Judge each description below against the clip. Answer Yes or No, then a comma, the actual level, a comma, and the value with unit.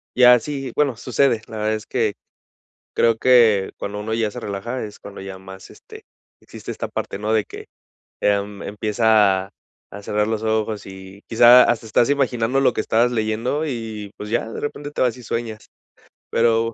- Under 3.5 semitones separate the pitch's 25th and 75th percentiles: Yes, narrow, 2.6 semitones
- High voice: No, low, 110 Hz